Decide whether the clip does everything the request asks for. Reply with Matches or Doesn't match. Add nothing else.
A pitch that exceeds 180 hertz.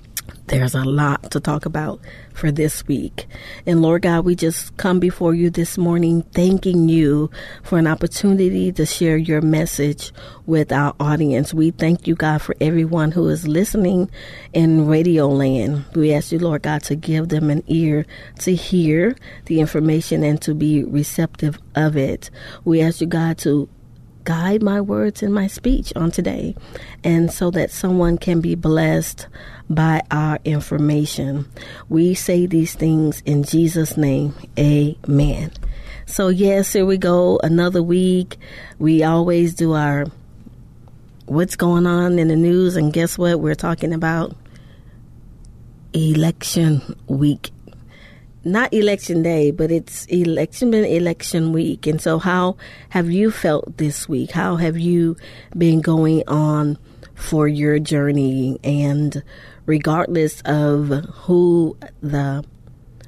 Doesn't match